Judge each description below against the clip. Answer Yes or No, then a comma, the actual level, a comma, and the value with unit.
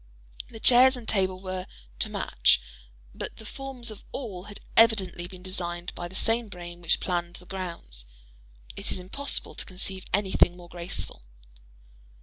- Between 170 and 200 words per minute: No, average, 155 wpm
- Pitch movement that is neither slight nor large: Yes, average, 3.9 semitones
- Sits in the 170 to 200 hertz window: Yes, medium, 185 Hz